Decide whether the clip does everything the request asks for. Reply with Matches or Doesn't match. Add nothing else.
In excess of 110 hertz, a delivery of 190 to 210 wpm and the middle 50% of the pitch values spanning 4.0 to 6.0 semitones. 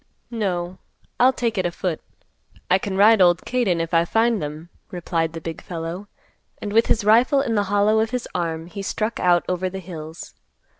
Matches